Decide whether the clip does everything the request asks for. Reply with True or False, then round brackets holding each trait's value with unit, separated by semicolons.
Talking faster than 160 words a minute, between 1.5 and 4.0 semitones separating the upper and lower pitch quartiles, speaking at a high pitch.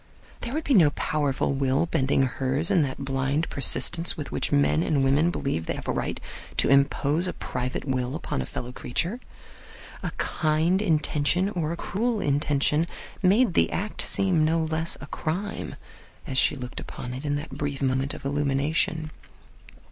False (170 wpm; 3.7 semitones; 145 Hz)